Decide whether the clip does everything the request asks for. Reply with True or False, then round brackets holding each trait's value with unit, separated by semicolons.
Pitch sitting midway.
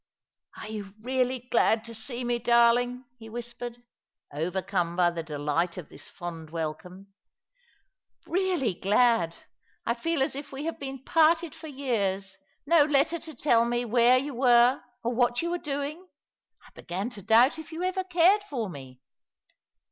False (240 Hz)